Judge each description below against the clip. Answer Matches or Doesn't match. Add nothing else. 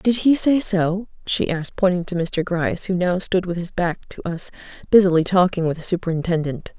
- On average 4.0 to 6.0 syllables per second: Matches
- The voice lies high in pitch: Doesn't match